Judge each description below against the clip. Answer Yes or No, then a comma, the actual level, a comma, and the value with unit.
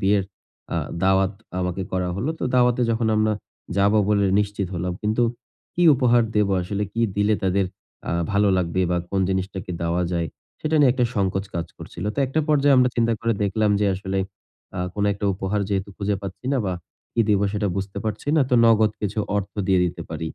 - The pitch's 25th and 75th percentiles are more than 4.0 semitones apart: No, average, 2.9 semitones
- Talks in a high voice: No, low, 100 Hz